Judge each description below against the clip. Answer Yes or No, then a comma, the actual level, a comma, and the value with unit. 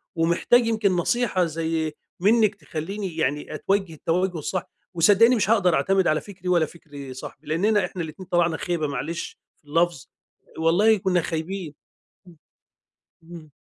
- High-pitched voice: No, medium, 175 Hz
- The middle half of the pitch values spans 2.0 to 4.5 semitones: Yes, average, 3.4 semitones